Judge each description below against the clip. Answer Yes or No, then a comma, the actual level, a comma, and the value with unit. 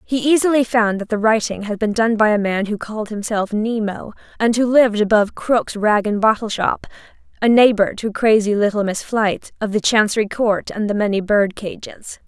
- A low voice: No, high, 215 Hz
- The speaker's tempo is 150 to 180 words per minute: No, average, 200 wpm